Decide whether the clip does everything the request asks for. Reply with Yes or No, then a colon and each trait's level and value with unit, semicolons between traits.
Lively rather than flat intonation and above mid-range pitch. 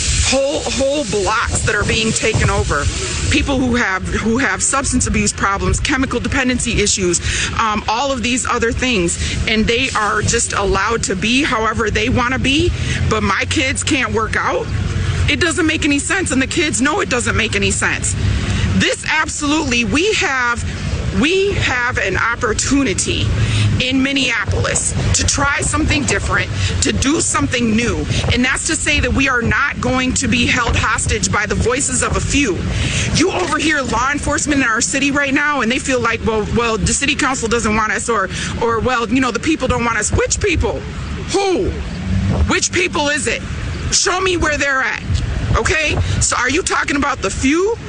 Yes: wide, 8.1 semitones; very high, 255 Hz